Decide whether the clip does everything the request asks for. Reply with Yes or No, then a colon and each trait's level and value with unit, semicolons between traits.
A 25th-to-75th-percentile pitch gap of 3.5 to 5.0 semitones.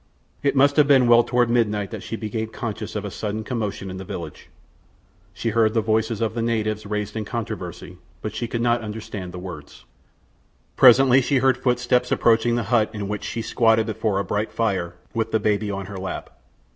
No: narrow, 2.5 semitones